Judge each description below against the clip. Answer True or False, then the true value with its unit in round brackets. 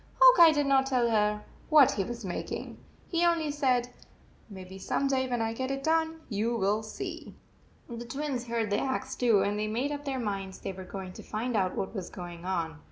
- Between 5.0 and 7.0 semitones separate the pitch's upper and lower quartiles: True (5.3 semitones)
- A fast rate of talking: True (220 wpm)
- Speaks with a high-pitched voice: True (235 Hz)